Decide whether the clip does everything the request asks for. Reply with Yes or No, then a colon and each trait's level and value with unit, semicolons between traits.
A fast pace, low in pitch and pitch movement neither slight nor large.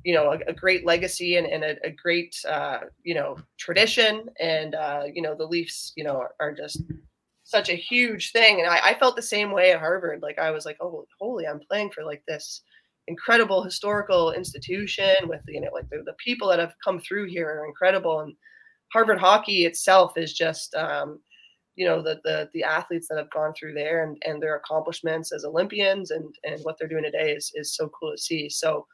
No: fast, 220 wpm; medium, 170 Hz; average, 4.8 semitones